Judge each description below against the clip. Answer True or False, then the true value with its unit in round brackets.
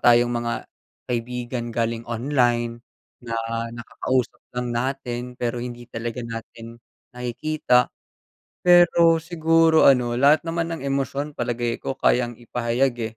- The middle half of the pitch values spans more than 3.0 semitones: False (2.7 semitones)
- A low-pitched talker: True (125 Hz)